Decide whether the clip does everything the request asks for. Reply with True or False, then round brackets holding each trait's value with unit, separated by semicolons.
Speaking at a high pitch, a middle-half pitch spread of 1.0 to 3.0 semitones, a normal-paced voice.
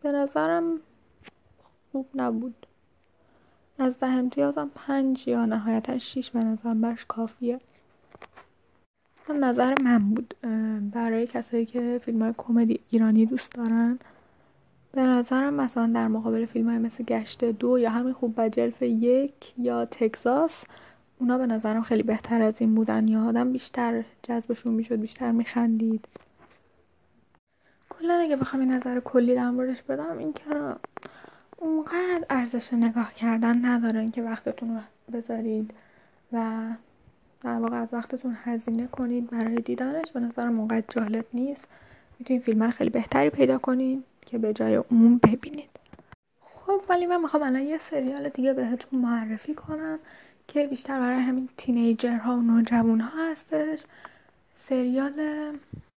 True (245 Hz; 2.7 semitones; 135 wpm)